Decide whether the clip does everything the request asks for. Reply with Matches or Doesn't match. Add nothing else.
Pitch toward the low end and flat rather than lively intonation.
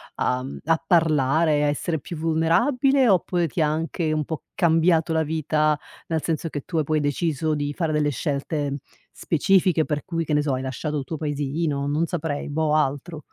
Doesn't match